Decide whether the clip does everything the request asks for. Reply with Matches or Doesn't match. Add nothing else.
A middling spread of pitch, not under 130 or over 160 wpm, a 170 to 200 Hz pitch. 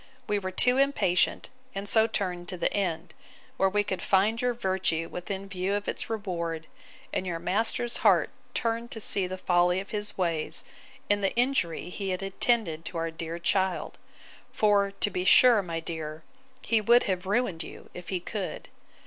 Doesn't match